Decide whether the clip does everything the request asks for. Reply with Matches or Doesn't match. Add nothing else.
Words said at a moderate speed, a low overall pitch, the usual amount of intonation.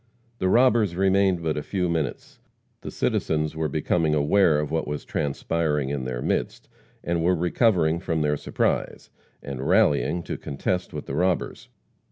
Matches